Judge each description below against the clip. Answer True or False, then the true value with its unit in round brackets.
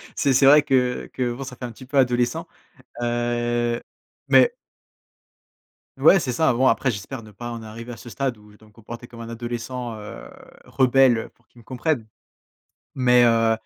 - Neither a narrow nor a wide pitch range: False (1.9 semitones)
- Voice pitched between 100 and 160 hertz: True (120 Hz)